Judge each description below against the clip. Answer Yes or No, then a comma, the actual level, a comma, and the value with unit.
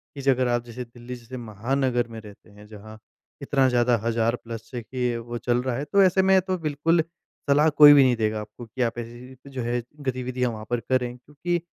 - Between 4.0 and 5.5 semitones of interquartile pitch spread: No, average, 2.8 semitones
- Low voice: Yes, low, 125 Hz